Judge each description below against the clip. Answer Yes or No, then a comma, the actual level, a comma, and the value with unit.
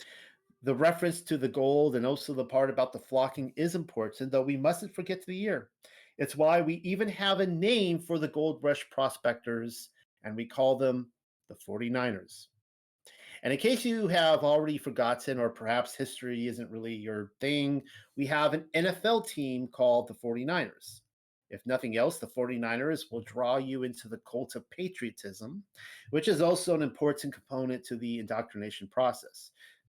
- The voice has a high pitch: No, low, 135 Hz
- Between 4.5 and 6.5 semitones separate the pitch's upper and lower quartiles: Yes, average, 4.9 semitones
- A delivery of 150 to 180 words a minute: Yes, average, 165 wpm